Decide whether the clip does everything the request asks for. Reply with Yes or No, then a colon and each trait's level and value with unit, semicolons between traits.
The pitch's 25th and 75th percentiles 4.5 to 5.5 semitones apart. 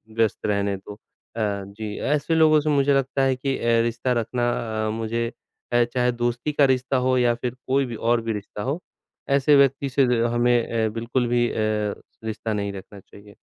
No: average, 3.4 semitones